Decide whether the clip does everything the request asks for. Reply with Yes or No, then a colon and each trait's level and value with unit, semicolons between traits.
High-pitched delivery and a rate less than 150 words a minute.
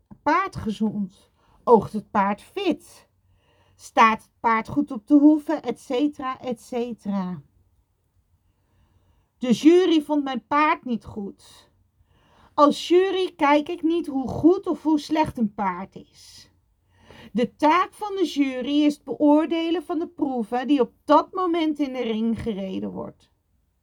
Yes: high, 240 Hz; average, 140 wpm